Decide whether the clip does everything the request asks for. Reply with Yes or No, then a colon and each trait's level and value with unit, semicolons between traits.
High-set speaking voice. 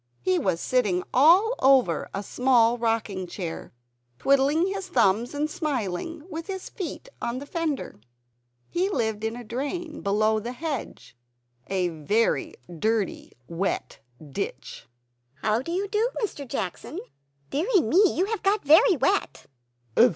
Yes: very high, 255 Hz